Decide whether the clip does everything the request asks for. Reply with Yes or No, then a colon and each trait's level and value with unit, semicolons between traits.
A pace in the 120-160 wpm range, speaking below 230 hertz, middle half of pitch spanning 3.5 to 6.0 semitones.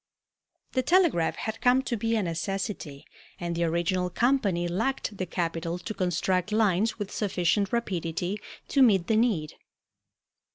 Yes: average, 140 wpm; high, 190 Hz; average, 4.6 semitones